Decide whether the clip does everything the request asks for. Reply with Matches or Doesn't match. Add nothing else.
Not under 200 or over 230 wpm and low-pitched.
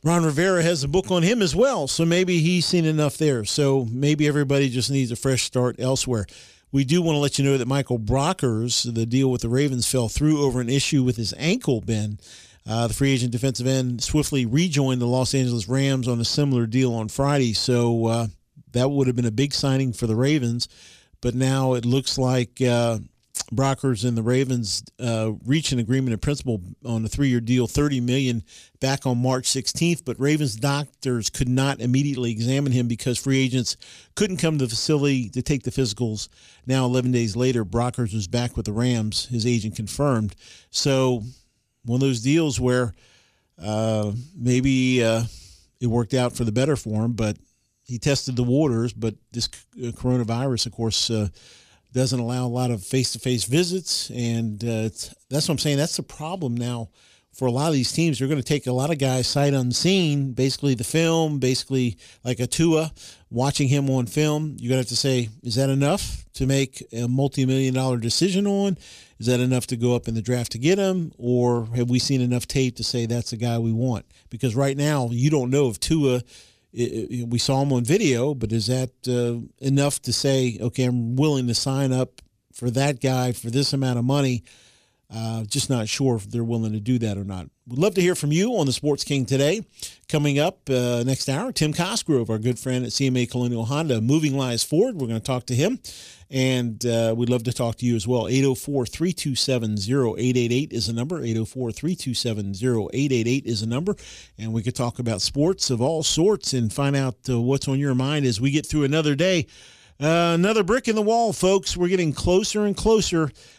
Matches